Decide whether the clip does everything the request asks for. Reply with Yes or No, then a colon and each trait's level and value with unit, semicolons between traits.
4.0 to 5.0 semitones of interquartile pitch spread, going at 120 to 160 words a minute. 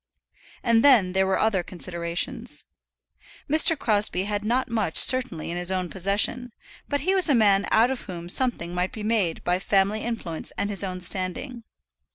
No: average, 4.6 semitones; average, 175 wpm